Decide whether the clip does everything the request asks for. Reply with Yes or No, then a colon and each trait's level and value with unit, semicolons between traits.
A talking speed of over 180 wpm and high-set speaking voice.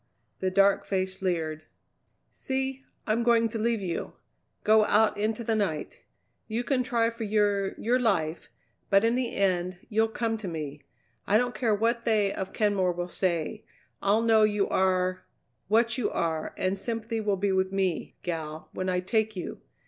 No: average, 170 wpm; high, 205 Hz